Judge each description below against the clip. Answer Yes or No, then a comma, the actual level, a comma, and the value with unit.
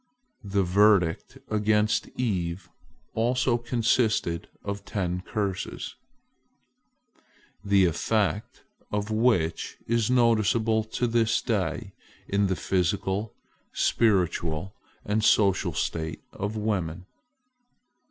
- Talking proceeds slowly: Yes, slow, 90 wpm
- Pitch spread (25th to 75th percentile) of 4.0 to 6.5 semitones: No, average, 3.2 semitones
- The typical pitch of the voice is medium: No, low, 105 Hz